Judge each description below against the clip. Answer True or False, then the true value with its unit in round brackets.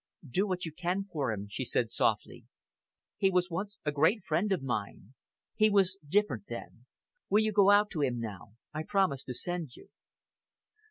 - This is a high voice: False (175 Hz)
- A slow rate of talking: False (180 wpm)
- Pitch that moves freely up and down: True (7.4 semitones)